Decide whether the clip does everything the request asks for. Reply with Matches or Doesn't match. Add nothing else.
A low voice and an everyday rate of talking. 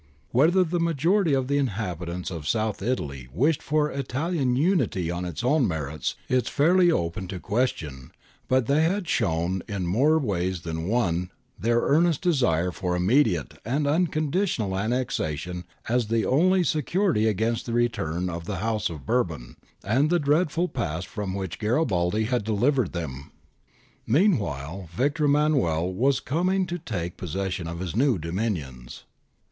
Matches